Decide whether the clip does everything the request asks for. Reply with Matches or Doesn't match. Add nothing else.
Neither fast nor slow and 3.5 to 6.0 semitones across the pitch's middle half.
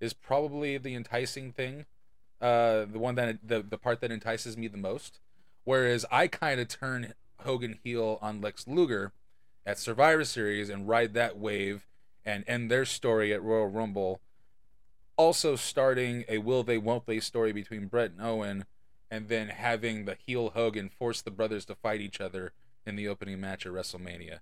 Doesn't match